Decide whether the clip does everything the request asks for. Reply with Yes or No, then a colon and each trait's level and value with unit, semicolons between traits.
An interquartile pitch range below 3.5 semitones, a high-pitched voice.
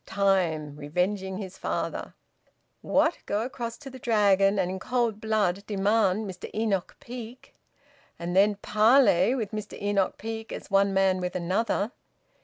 Yes: average, 2.9 semitones; high, 200 Hz